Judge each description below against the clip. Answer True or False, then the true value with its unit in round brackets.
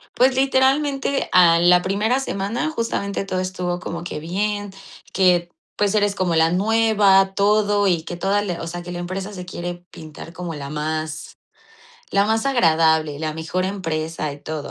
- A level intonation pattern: False (3.6 semitones)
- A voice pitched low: False (185 Hz)